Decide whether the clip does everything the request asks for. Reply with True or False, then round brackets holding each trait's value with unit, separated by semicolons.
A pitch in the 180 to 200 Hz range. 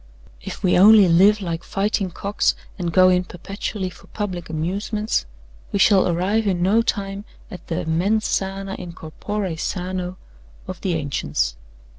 True (185 Hz)